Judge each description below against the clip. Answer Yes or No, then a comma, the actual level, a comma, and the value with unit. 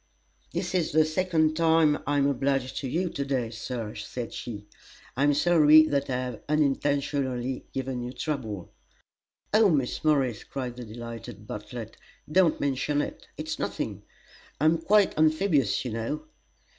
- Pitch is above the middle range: No, medium, 140 Hz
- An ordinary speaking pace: Yes, average, 155 wpm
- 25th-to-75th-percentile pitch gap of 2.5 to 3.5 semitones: No, average, 4.2 semitones